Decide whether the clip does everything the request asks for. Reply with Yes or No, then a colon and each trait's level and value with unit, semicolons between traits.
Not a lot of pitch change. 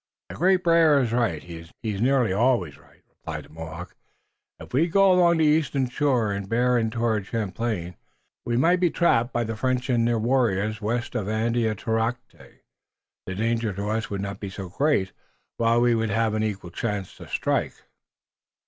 No: average, 3.8 semitones